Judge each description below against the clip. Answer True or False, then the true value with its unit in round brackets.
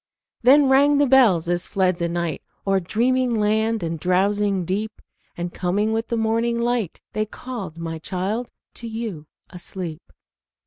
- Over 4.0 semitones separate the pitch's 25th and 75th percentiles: True (4.8 semitones)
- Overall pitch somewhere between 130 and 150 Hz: False (210 Hz)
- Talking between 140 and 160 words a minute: True (150 wpm)